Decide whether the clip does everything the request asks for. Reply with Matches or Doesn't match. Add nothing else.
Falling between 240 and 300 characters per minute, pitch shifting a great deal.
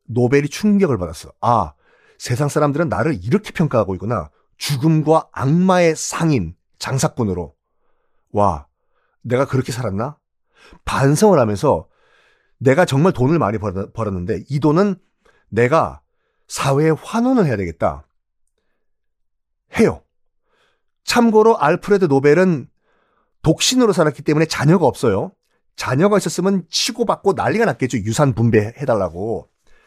Matches